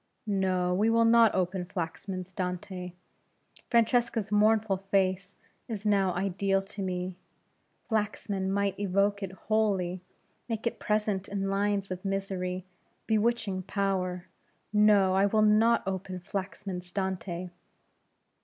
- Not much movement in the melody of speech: Yes, narrow, 2.2 semitones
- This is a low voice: No, high, 195 Hz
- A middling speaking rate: No, slow, 115 wpm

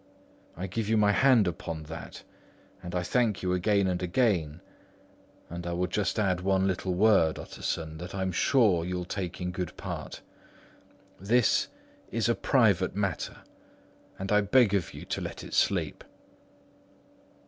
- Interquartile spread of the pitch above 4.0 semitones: No, average, 2.9 semitones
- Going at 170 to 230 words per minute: No, average, 155 wpm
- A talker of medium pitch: No, very low, 95 Hz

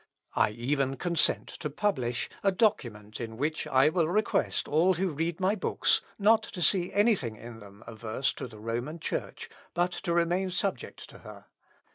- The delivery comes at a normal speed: Yes, average, 175 wpm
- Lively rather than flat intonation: Yes, wide, 7.7 semitones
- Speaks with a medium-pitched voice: Yes, medium, 155 Hz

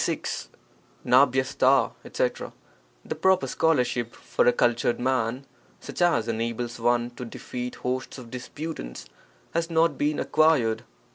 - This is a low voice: Yes, low, 125 Hz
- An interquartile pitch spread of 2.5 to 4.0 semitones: Yes, average, 3.6 semitones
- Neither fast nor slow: No, slow, 115 wpm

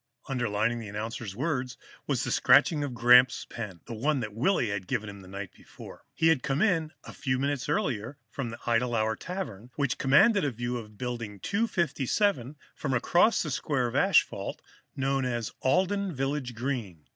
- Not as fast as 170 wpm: No, average, 180 wpm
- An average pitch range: Yes, average, 4.5 semitones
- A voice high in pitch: No, low, 125 Hz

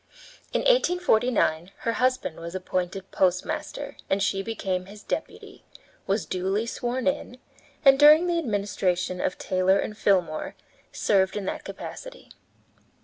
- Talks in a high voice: Yes, high, 200 Hz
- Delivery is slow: Yes, slow, 130 wpm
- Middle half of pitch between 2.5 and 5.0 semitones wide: No, wide, 5.5 semitones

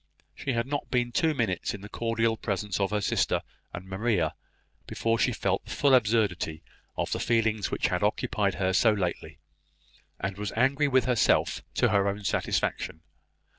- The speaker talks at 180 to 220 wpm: No, average, 170 wpm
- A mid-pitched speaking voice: No, low, 110 Hz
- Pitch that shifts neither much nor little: Yes, average, 3.6 semitones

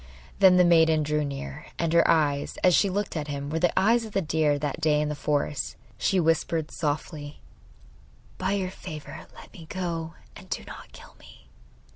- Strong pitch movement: No, average, 3.2 semitones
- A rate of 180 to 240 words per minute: Yes, average, 190 wpm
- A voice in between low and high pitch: Yes, medium, 160 Hz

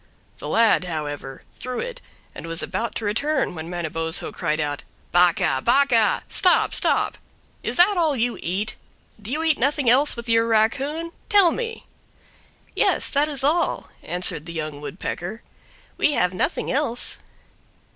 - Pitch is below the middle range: No, high, 230 Hz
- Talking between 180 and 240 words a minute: No, average, 150 wpm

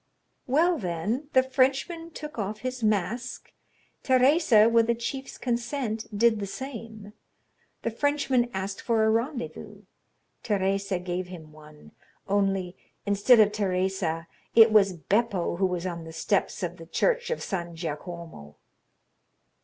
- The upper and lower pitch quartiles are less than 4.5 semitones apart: No, wide, 5.5 semitones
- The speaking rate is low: Yes, slow, 130 wpm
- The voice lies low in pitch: No, high, 210 Hz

